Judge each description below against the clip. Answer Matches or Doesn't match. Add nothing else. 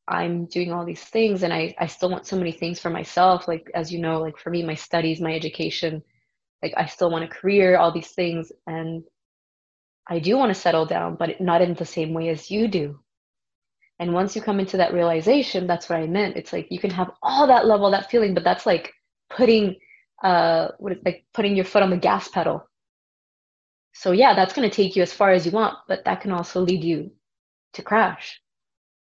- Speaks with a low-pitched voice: Doesn't match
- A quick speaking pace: Matches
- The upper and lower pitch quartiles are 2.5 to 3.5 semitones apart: Matches